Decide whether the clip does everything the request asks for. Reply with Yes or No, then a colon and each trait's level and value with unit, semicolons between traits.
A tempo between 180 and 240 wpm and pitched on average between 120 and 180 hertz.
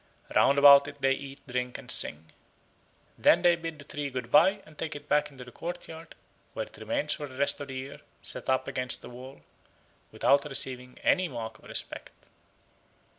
Yes: average, 190 wpm; medium, 140 Hz